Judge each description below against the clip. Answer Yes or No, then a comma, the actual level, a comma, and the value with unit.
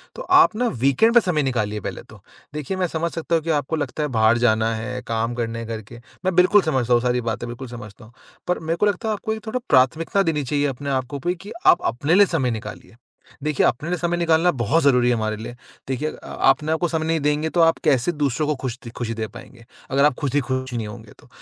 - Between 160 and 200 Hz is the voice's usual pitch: No, medium, 140 Hz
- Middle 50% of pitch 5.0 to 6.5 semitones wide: Yes, wide, 5.6 semitones